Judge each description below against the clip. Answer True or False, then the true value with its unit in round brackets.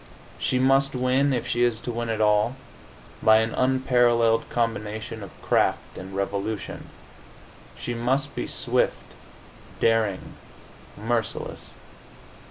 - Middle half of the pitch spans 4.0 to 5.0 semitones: False (2.6 semitones)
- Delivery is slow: True (115 wpm)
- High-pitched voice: False (115 Hz)